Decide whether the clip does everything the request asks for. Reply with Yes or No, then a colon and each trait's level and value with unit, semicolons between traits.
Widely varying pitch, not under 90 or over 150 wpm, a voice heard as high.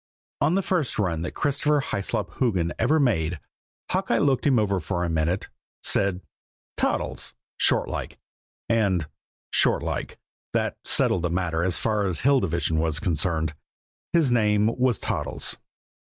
No: wide, 6.6 semitones; average, 140 wpm; low, 100 Hz